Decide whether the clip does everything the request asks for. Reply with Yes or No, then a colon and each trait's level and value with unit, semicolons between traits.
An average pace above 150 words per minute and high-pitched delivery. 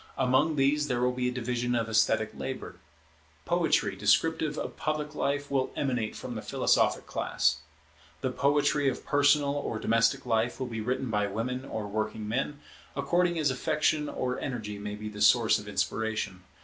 No: average, 170 wpm; low, 125 Hz